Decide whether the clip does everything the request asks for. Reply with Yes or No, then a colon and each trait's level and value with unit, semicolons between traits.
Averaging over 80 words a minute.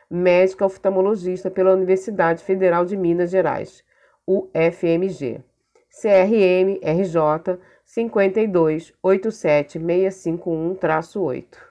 No: slow, 60 wpm